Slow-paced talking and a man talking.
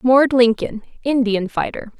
No: slow, 120 wpm; female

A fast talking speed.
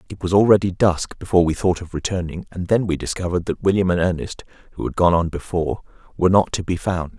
Yes: fast, 225 wpm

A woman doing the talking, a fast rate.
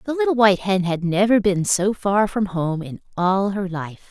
Yes: female; fast, 220 wpm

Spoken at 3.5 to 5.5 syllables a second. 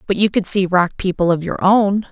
Yes: 5.2 syllables/s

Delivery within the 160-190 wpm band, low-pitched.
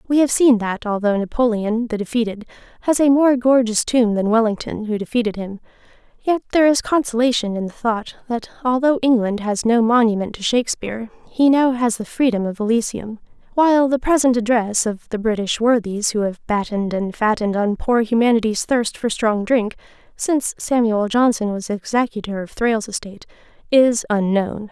No: average, 170 wpm; high, 230 Hz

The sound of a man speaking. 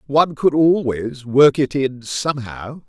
Yes: male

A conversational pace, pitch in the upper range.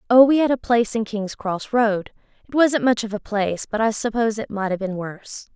No: fast, 240 wpm; high, 220 Hz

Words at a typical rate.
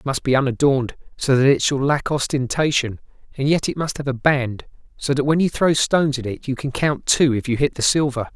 No: fast, 245 wpm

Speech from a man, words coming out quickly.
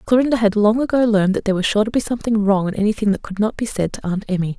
No: female; fast, 300 wpm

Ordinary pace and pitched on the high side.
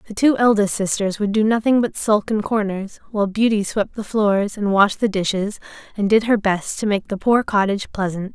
No: fast, 215 wpm; high, 205 Hz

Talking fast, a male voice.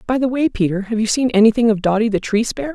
No: fast, 285 wpm; female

